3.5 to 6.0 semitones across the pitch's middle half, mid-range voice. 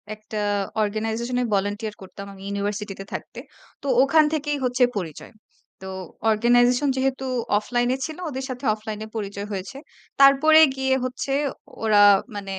No: average, 4.5 semitones; high, 225 Hz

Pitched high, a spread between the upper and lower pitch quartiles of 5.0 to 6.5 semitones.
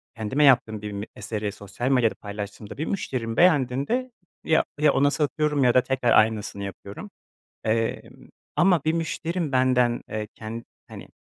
No: low, 125 Hz; average, 5.3 semitones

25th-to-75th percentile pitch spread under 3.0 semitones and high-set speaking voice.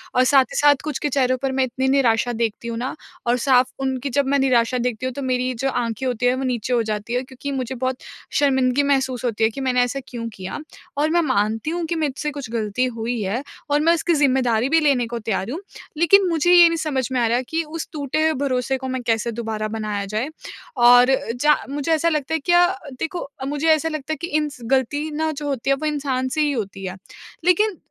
No: average, 3.7 semitones; very high, 260 Hz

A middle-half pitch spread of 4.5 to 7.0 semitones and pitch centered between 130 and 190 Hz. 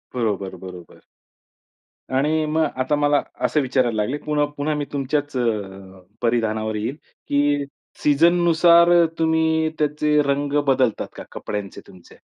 Yes: average, 5.1 semitones; medium, 140 Hz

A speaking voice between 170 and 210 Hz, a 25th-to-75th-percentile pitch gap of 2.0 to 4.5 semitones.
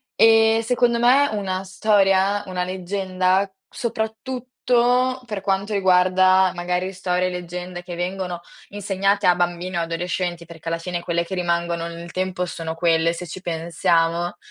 Yes: medium, 185 Hz; narrow, 2.5 semitones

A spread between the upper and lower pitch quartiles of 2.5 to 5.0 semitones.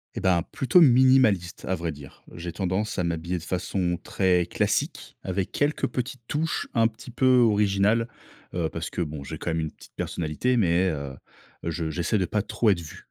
No: wide, 5.4 semitones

